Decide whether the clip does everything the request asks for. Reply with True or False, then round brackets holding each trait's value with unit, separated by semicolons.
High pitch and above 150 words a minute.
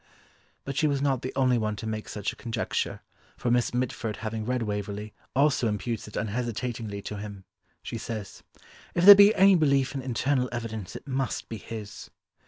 False (120 Hz; 185 wpm)